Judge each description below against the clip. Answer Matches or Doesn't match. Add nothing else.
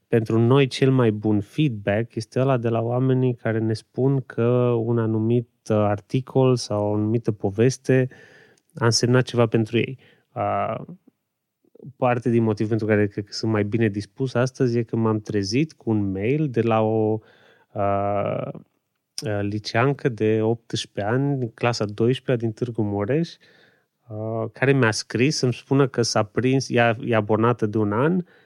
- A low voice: Matches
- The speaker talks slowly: Doesn't match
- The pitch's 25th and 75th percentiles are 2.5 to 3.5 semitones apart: Matches